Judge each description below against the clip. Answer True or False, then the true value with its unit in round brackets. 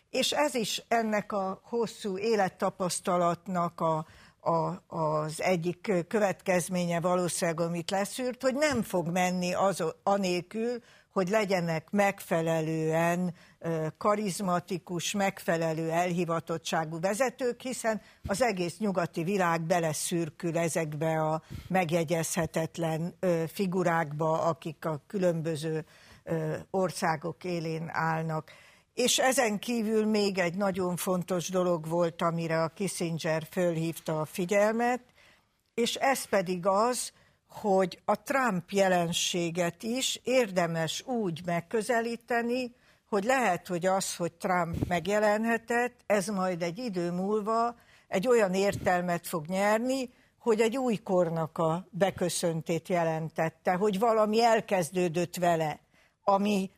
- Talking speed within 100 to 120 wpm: True (105 wpm)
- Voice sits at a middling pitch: True (180 Hz)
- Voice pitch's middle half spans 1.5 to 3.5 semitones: False (3.9 semitones)